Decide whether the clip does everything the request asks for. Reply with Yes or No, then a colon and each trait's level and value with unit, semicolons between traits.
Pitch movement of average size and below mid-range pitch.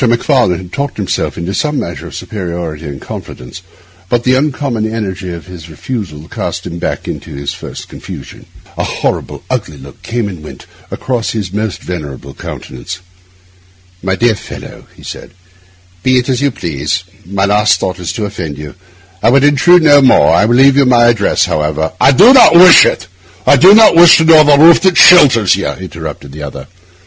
No: wide, 7.8 semitones; low, 100 Hz